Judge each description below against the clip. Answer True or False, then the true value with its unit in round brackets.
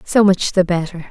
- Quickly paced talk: True (215 wpm)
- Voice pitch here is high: False (180 Hz)